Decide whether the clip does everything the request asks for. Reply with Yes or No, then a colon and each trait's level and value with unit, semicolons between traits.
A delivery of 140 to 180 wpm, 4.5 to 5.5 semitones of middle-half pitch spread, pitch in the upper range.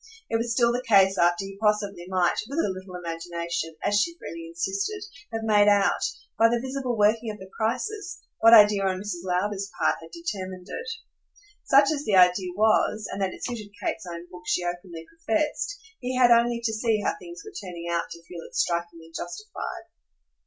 No: average, 195 wpm; average, 5.0 semitones; high, 205 Hz